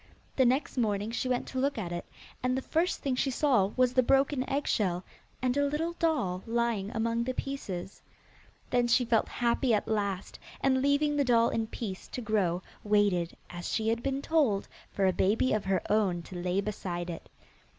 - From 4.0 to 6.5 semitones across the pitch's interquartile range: Yes, average, 5.0 semitones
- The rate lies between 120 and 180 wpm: No, average, 190 wpm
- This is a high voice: Yes, high, 230 Hz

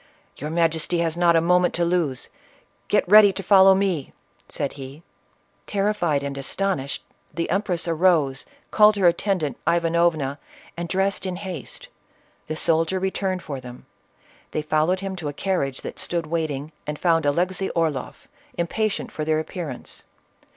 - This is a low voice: No, medium, 170 Hz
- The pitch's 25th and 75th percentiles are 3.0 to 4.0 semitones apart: Yes, average, 3.6 semitones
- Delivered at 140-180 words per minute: Yes, average, 150 wpm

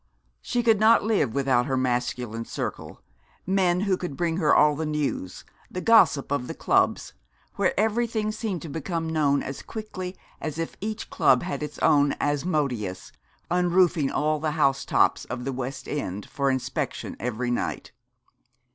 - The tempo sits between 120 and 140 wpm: No, average, 155 wpm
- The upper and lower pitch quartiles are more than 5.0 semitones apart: Yes, wide, 5.5 semitones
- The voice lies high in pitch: No, medium, 150 Hz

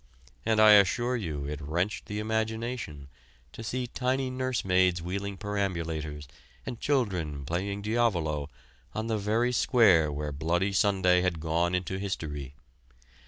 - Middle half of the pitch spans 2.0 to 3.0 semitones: No, wide, 5.6 semitones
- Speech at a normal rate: No, slow, 130 wpm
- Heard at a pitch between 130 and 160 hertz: No, very low, 95 Hz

